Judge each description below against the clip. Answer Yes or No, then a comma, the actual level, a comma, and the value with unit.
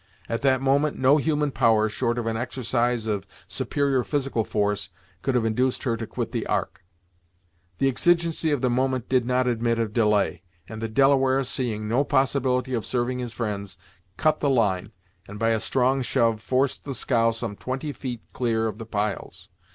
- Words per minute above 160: Yes, average, 180 wpm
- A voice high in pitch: No, low, 125 Hz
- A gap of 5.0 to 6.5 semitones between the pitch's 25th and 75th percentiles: No, average, 3.1 semitones